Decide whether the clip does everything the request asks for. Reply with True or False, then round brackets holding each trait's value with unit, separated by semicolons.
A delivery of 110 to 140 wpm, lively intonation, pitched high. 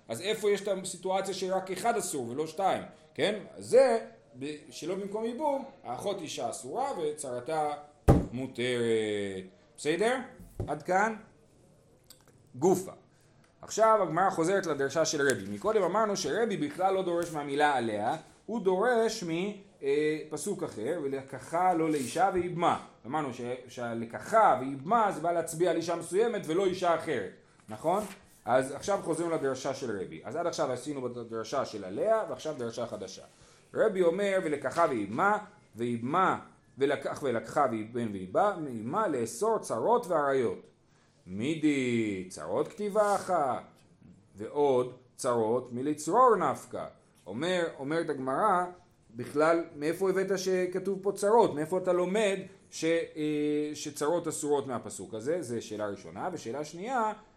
False (125 wpm; 6.3 semitones; 160 Hz)